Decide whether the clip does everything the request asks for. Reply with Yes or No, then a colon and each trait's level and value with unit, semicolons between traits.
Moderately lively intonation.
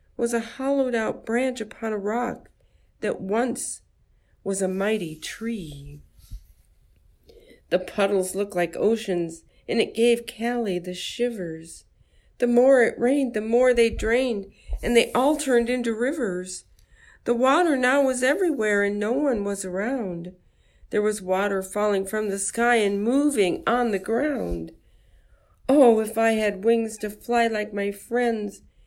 Yes: average, 3.5 semitones